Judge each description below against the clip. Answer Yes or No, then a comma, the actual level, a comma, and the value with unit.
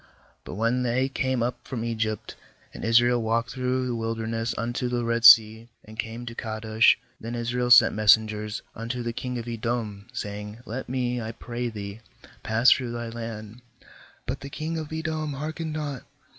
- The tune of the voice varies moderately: No, narrow, 2.0 semitones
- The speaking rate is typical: Yes, average, 180 wpm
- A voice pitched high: No, low, 120 Hz